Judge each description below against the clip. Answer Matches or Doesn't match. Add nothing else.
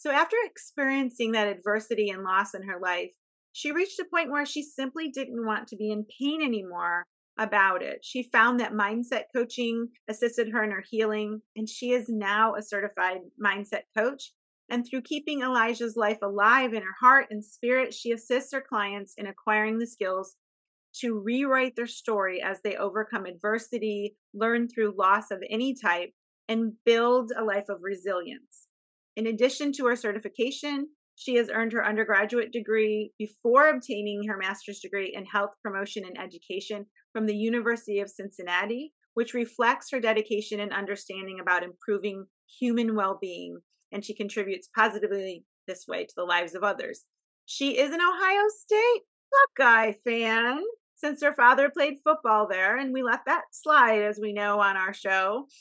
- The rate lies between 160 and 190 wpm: Matches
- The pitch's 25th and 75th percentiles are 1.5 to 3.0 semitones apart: Doesn't match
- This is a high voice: Matches